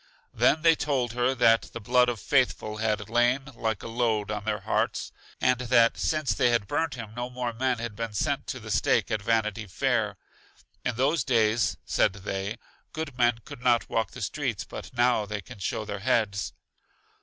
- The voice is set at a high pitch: No, low, 115 Hz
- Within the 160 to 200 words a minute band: Yes, average, 190 wpm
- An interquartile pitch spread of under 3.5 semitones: Yes, average, 2.7 semitones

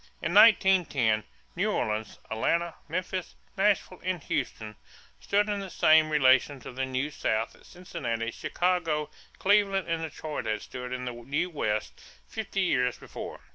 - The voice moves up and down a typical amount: No, wide, 6.7 semitones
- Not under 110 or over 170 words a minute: Yes, average, 145 wpm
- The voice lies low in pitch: No, medium, 155 Hz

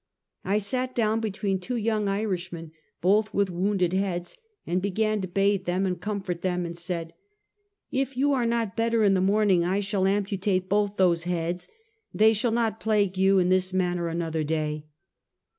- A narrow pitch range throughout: No, average, 3.1 semitones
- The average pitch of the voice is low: No, high, 195 Hz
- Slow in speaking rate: No, average, 180 wpm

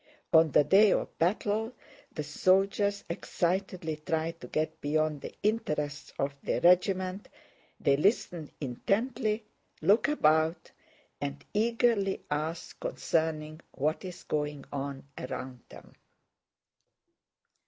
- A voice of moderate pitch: Yes, medium, 165 Hz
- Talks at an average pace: No, slow, 110 wpm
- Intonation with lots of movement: No, average, 4.8 semitones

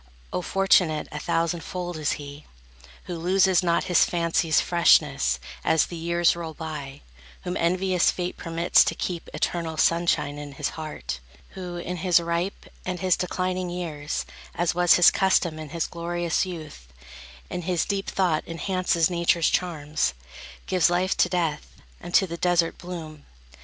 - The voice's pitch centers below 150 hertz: No, medium, 170 Hz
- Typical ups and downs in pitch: No, narrow, 2.2 semitones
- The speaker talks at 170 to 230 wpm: No, average, 155 wpm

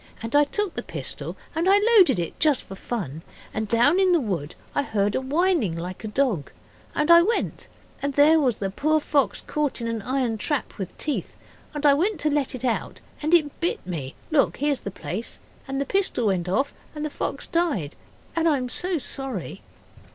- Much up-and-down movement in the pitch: Yes, wide, 6.5 semitones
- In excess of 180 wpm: Yes, fast, 205 wpm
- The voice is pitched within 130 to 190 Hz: No, very high, 275 Hz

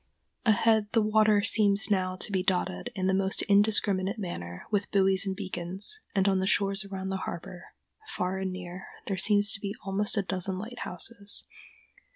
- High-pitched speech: Yes, high, 195 Hz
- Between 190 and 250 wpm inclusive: No, average, 175 wpm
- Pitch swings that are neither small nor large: No, narrow, 1.7 semitones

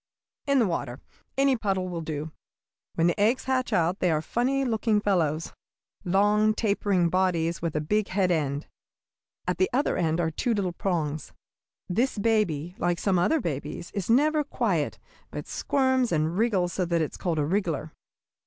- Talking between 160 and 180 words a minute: Yes, average, 170 wpm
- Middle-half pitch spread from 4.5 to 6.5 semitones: Yes, average, 5.1 semitones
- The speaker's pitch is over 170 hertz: Yes, medium, 185 Hz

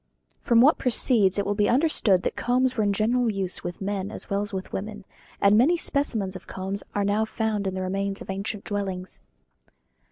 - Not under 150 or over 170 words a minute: No, average, 200 wpm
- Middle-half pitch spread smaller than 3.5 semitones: Yes, average, 2.8 semitones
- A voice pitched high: Yes, high, 205 Hz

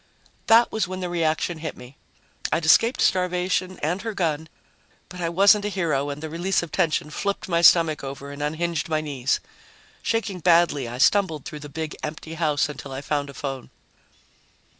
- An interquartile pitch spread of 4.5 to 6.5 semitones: No, average, 3.7 semitones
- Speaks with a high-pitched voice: No, medium, 160 Hz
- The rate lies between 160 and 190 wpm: Yes, average, 185 wpm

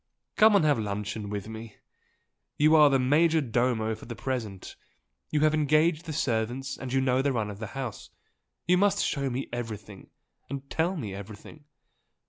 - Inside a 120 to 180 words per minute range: Yes, average, 175 wpm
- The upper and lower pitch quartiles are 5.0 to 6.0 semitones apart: Yes, wide, 5.5 semitones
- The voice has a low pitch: Yes, low, 130 Hz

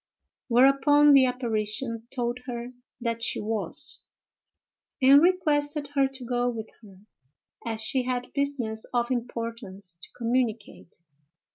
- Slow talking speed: Yes, slow, 120 wpm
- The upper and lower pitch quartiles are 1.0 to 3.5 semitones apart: Yes, average, 3.2 semitones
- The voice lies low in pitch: No, high, 245 Hz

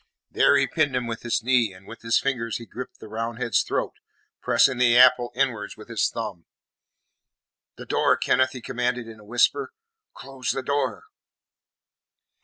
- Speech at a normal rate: Yes, average, 165 wpm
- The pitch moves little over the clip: Yes, narrow, 2.1 semitones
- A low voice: Yes, low, 120 Hz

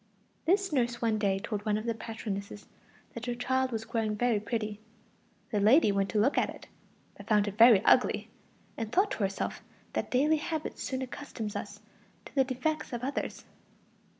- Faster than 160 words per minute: Yes, average, 180 wpm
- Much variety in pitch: No, average, 3.8 semitones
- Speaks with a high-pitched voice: Yes, high, 230 Hz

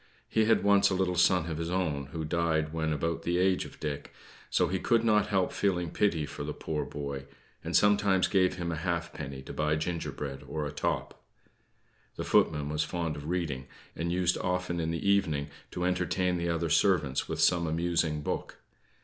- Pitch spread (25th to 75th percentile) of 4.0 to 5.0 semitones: No, average, 3.1 semitones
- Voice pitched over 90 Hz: No, very low, 85 Hz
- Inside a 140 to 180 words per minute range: No, average, 190 wpm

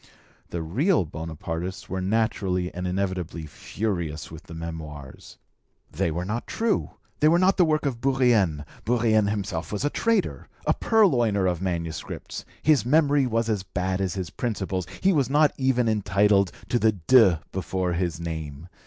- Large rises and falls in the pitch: Yes, wide, 6.3 semitones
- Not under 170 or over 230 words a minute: No, average, 160 wpm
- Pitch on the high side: No, very low, 95 Hz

